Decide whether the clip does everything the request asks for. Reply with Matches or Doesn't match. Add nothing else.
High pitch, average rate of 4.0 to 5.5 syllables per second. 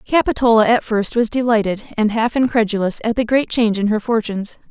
Doesn't match